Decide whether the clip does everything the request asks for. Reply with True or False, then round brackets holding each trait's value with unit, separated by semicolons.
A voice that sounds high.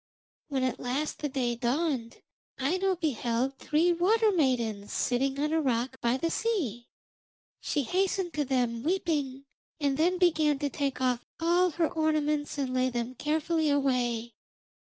True (285 Hz)